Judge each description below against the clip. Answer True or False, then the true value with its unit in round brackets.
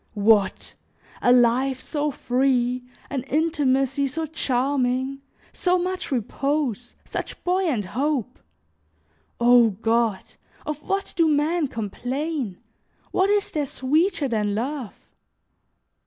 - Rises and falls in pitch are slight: False (3.9 semitones)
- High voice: True (270 Hz)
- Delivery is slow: True (105 wpm)